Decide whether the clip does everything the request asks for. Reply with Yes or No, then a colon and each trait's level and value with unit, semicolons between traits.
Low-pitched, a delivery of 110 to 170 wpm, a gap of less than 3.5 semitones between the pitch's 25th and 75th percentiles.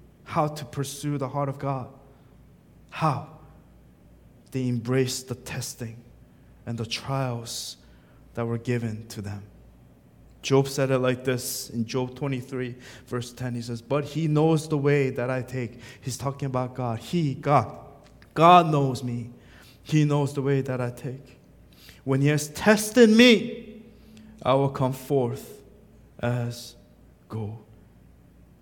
Yes: low, 130 Hz; average, 140 wpm; average, 2.9 semitones